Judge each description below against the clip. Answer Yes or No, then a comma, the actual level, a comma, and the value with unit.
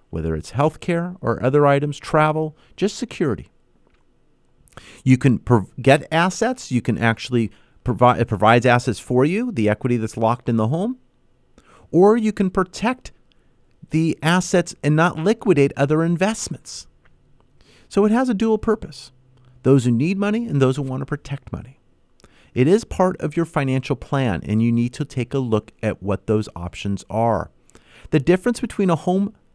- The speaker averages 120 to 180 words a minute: Yes, average, 165 wpm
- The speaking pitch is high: No, medium, 140 Hz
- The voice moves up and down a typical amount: No, wide, 7.4 semitones